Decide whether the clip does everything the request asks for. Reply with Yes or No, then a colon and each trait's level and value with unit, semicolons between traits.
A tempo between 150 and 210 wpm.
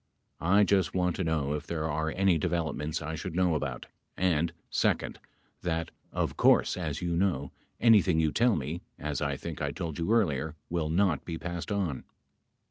Yes: average, 180 wpm